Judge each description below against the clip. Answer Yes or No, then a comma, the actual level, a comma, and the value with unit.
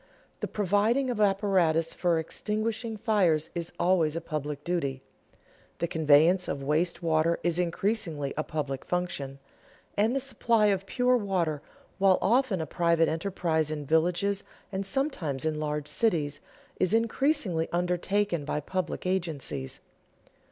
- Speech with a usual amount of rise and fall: Yes, average, 4.5 semitones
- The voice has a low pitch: No, medium, 175 Hz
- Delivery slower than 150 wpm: Yes, slow, 135 wpm